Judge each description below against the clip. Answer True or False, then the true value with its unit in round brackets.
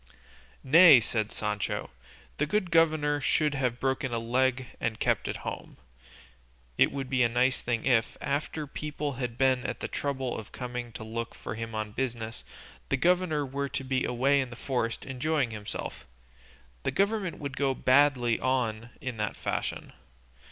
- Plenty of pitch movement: False (3.5 semitones)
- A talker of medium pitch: False (130 Hz)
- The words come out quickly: False (165 wpm)